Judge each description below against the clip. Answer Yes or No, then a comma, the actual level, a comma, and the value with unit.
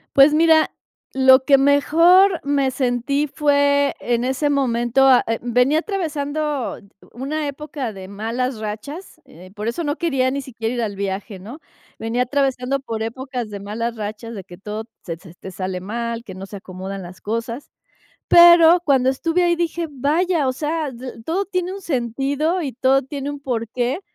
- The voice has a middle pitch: No, very high, 260 Hz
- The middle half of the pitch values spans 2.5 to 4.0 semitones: No, average, 4.6 semitones